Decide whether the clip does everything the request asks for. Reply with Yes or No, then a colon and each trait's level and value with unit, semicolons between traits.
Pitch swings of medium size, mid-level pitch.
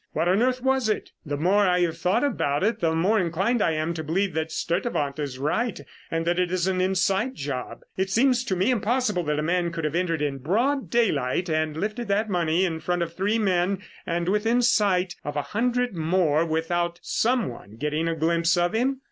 Yes: average, 4.8 semitones; medium, 180 Hz